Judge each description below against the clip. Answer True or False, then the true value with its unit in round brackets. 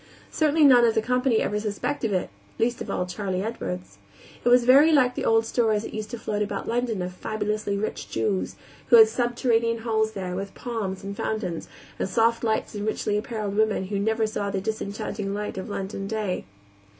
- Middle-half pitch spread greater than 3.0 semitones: False (2.6 semitones)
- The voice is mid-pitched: False (215 Hz)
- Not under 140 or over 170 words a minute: False (195 wpm)